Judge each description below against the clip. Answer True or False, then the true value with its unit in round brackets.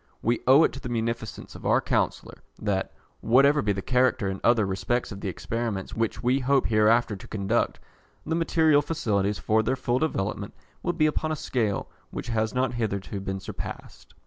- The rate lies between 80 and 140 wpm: False (185 wpm)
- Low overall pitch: True (115 Hz)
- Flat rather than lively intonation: False (4.2 semitones)